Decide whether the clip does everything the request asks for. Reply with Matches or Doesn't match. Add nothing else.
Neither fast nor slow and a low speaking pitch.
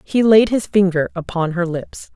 Doesn't match